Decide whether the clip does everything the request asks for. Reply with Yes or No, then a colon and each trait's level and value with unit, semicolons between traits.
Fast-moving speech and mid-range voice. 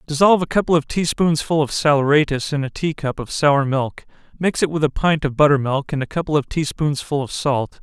Yes: fast, 230 wpm; medium, 150 Hz